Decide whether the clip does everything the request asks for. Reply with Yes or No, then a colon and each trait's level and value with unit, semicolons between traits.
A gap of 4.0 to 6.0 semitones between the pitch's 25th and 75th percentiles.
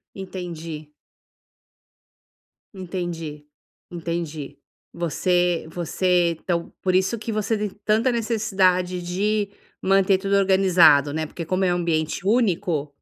No: average, 2.8 semitones